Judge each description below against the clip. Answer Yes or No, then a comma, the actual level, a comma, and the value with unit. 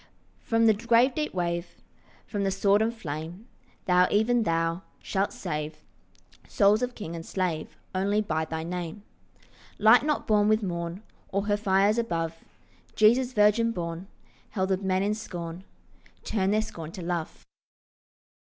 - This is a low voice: No, high, 195 Hz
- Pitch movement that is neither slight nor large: Yes, average, 4.1 semitones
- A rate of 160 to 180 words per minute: No, average, 150 wpm